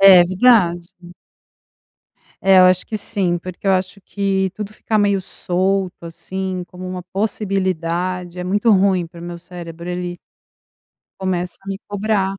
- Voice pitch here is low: No, medium, 185 Hz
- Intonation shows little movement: Yes, narrow, 1.7 semitones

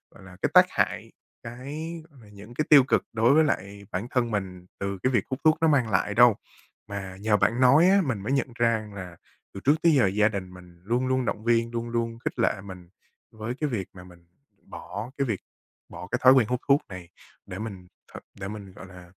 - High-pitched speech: No, low, 110 Hz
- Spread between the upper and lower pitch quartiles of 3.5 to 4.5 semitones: No, average, 4.9 semitones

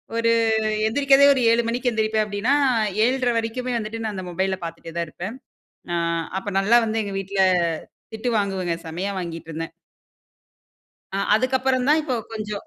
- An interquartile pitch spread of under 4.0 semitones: No, average, 4.5 semitones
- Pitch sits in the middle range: No, high, 220 Hz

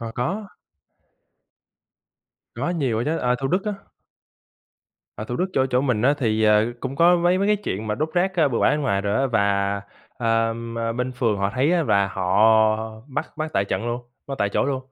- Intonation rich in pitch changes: Yes, wide, 6.2 semitones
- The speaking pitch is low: Yes, low, 125 Hz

